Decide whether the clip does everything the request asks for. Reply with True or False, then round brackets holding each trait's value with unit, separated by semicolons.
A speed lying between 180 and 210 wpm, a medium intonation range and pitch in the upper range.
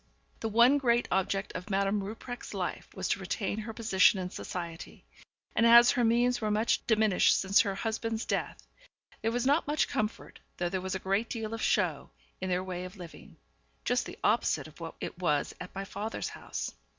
True (195 wpm; 3.6 semitones; 210 Hz)